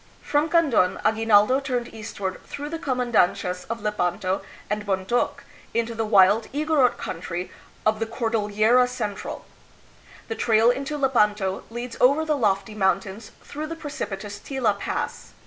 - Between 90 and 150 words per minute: Yes, average, 140 wpm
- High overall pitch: Yes, high, 225 Hz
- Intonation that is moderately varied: Yes, average, 4.3 semitones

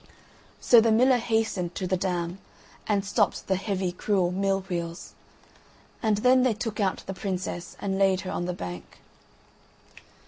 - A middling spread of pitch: Yes, average, 3.1 semitones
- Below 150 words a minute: No, average, 160 wpm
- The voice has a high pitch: Yes, high, 195 Hz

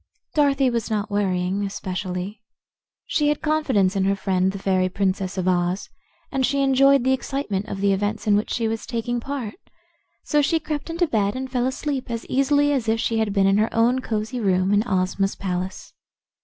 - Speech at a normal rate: Yes, average, 195 wpm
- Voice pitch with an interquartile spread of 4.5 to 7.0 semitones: Yes, average, 5.3 semitones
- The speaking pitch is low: No, high, 215 Hz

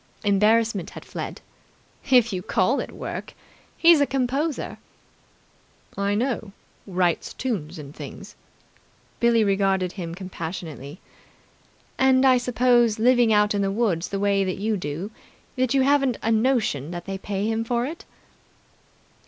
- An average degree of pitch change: Yes, average, 4.6 semitones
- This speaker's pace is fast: No, average, 140 wpm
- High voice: Yes, high, 210 Hz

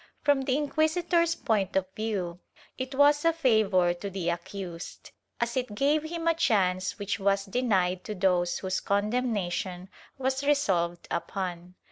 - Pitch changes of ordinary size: No, wide, 7.0 semitones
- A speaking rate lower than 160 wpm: Yes, average, 145 wpm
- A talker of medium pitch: No, high, 205 Hz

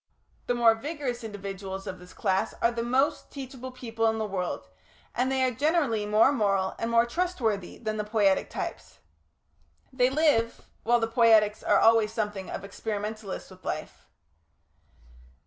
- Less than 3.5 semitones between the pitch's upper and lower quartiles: Yes, average, 3.1 semitones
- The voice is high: Yes, high, 225 Hz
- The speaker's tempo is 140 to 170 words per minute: Yes, average, 155 wpm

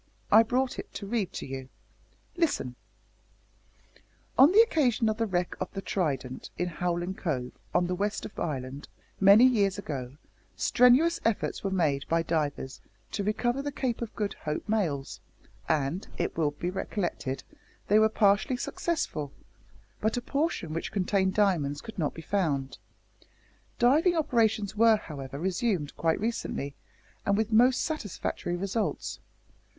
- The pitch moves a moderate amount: No, wide, 6.8 semitones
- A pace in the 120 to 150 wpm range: Yes, average, 145 wpm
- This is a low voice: No, high, 195 Hz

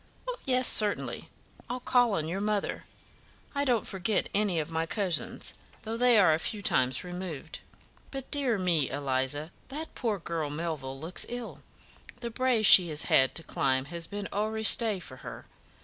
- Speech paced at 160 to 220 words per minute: Yes, average, 170 wpm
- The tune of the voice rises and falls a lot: Yes, wide, 6.4 semitones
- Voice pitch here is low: No, high, 190 Hz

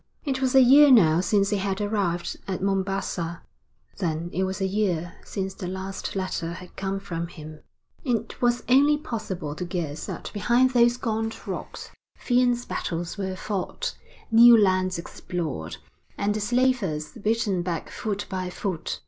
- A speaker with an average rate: Yes, average, 155 wpm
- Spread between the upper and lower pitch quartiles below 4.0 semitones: No, average, 4.4 semitones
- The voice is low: No, high, 195 Hz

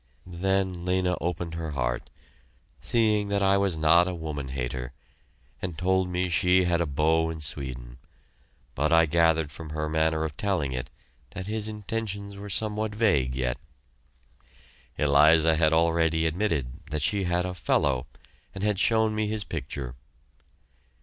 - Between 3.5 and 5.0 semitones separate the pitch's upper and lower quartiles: Yes, average, 4.1 semitones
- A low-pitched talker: Yes, very low, 85 Hz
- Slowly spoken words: No, average, 150 wpm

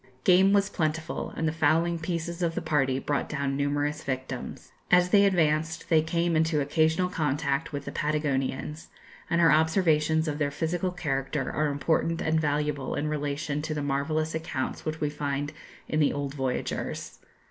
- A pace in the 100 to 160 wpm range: No, average, 170 wpm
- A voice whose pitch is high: No, medium, 155 Hz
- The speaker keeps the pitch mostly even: Yes, narrow, 2.2 semitones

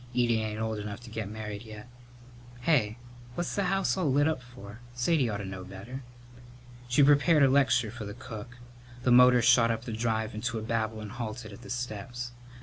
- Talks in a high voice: No, low, 115 Hz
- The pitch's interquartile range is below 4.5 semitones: Yes, average, 2.7 semitones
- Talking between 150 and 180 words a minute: No, average, 200 wpm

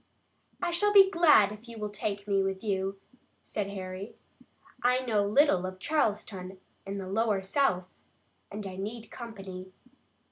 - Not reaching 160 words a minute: Yes, average, 150 wpm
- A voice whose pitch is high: Yes, high, 205 Hz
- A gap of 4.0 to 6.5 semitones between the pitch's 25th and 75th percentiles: No, average, 3.4 semitones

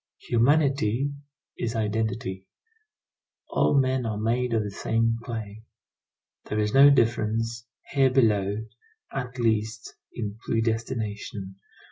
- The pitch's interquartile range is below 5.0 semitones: Yes, average, 2.7 semitones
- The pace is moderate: No, slow, 105 wpm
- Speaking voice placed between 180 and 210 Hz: No, low, 115 Hz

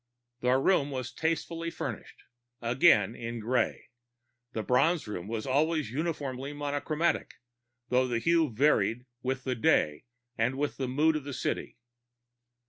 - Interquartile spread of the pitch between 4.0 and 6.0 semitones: Yes, average, 4.3 semitones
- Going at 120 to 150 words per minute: Yes, slow, 135 wpm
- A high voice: No, low, 130 Hz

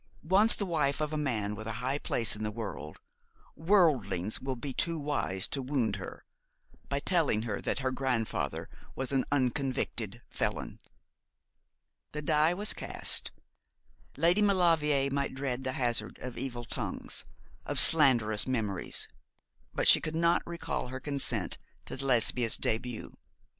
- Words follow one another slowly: No, average, 145 wpm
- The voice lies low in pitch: Yes, low, 130 Hz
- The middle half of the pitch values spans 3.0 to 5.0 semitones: Yes, average, 4.7 semitones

